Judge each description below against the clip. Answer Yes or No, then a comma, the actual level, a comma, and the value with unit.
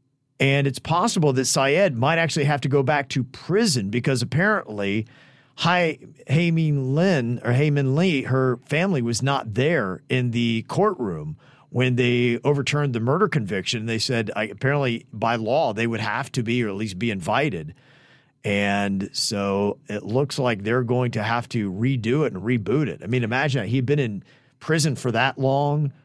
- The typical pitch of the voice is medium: No, low, 130 Hz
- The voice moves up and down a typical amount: Yes, average, 3.6 semitones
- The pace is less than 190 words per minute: Yes, average, 180 wpm